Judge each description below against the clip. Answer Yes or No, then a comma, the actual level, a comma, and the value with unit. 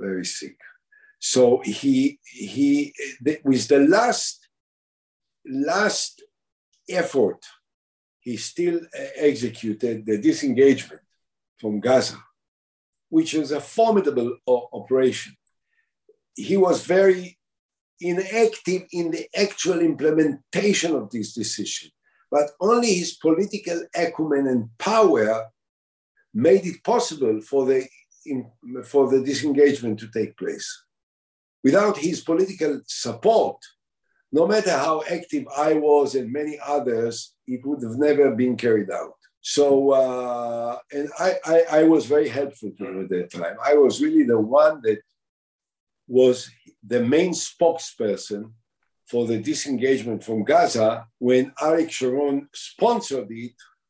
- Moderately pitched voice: Yes, medium, 145 Hz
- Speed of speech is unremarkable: No, slow, 120 wpm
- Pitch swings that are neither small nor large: No, wide, 6.8 semitones